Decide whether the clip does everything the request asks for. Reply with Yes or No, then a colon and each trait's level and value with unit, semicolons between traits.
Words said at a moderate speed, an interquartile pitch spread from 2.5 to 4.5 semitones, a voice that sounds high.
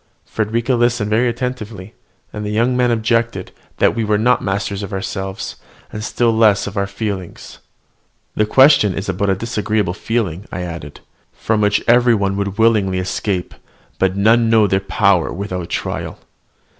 No: average, 170 wpm; average, 3.0 semitones; low, 105 Hz